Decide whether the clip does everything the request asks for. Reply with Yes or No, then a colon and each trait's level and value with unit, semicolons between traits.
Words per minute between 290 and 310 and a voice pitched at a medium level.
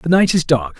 Yes: fast, 300 wpm; medium, 150 Hz